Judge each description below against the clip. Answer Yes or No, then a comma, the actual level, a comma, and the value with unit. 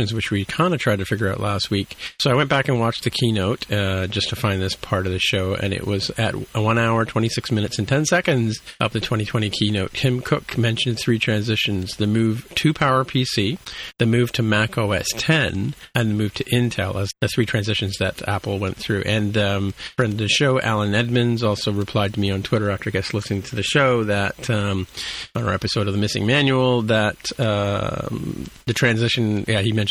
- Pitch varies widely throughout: No, average, 3.2 semitones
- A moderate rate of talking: No, fast, 215 wpm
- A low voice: Yes, low, 110 Hz